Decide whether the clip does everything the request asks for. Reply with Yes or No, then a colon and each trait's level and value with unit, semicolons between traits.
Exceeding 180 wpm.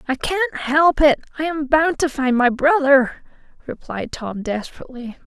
No: average, 145 wpm